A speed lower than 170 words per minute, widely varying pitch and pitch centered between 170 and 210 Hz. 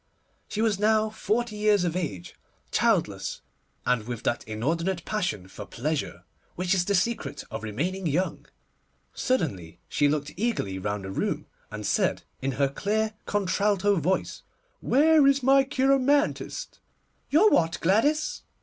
Yes: average, 140 wpm; wide, 8.1 semitones; medium, 185 Hz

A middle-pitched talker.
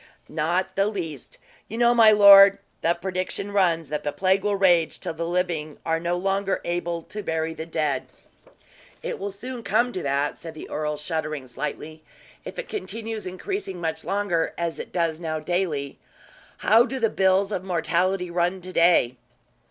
Yes: medium, 175 Hz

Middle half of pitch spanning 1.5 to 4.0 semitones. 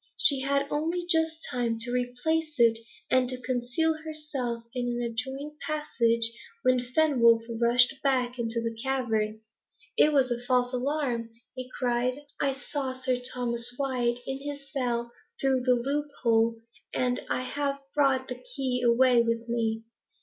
Yes: average, 2.7 semitones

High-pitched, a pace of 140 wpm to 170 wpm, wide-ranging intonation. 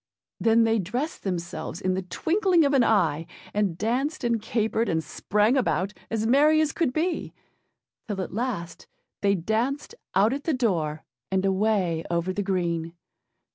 Yes: high, 210 Hz; average, 160 wpm; wide, 5.7 semitones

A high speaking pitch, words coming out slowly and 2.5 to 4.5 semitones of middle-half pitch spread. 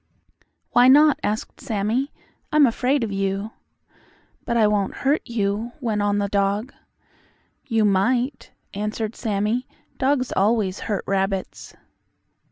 Yes: high, 215 Hz; slow, 120 wpm; average, 3.8 semitones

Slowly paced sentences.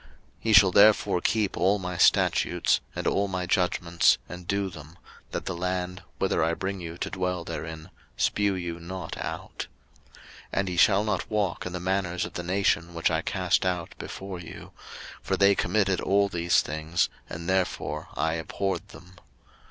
No: average, 175 wpm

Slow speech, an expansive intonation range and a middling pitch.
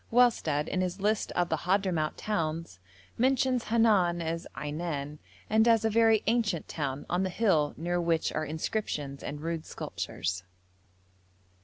No: average, 145 wpm; wide, 5.9 semitones; medium, 175 Hz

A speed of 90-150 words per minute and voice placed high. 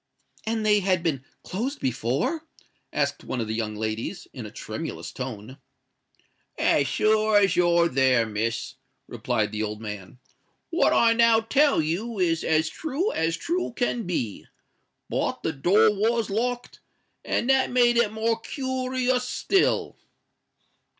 Yes: average, 140 wpm; high, 195 Hz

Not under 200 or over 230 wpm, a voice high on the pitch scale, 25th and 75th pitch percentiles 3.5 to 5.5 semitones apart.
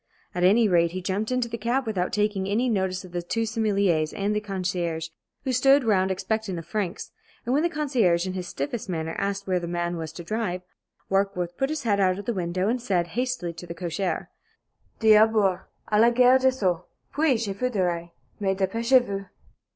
Yes: fast, 205 wpm; high, 195 Hz; average, 4.4 semitones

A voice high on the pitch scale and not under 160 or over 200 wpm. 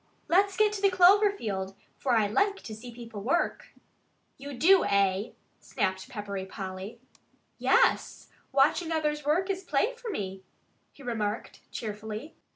No: very high, 250 Hz; average, 145 wpm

